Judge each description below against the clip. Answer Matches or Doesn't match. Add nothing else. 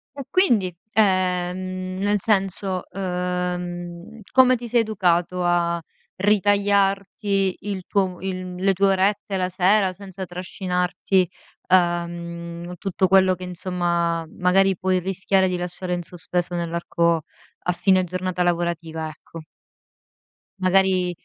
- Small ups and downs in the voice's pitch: Matches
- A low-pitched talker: Doesn't match